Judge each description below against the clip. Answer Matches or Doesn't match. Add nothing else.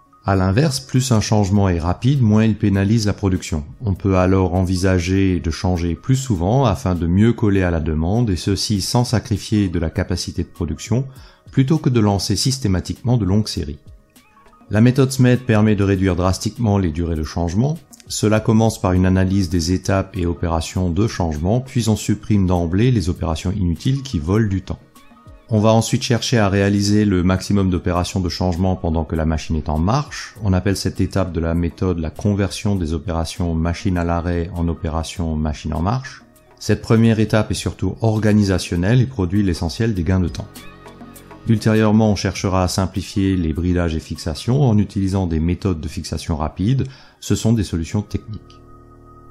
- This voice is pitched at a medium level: Doesn't match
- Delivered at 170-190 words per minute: Matches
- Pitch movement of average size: Matches